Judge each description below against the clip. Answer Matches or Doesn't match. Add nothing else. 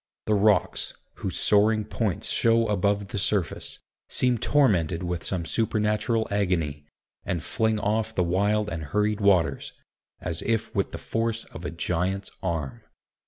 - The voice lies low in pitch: Matches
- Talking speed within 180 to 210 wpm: Doesn't match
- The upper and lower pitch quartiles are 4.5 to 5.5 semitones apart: Doesn't match